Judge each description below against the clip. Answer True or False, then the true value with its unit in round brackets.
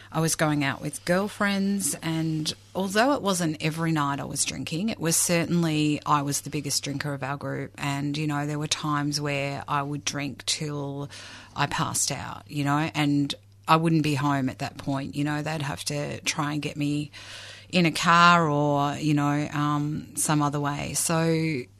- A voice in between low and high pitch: True (145 Hz)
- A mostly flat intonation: True (2.0 semitones)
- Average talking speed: True (195 wpm)